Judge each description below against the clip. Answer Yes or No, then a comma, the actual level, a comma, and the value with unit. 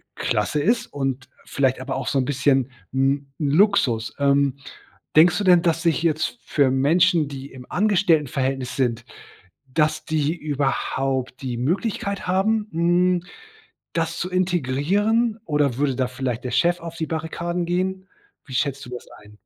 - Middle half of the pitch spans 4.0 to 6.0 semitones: Yes, average, 4.8 semitones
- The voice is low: No, medium, 150 Hz